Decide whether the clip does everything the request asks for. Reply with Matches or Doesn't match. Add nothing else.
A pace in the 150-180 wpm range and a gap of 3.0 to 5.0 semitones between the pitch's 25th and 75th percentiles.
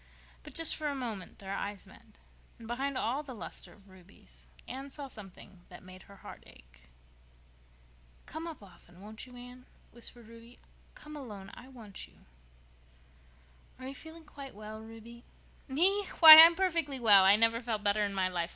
Doesn't match